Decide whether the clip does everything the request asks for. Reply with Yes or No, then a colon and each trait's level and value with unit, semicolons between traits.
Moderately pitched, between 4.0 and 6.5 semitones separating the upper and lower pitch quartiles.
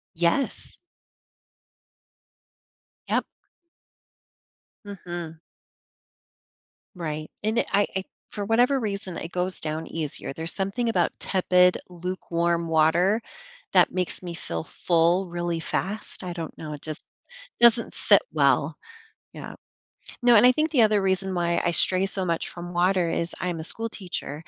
No: medium, 180 Hz; average, 2.9 semitones